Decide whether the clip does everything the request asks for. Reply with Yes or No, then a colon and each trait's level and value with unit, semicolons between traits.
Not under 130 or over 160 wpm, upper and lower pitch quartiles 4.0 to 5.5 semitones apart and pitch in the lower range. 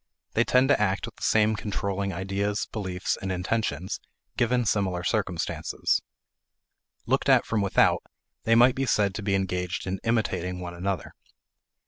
No: average, 150 wpm; average, 3.0 semitones; low, 100 Hz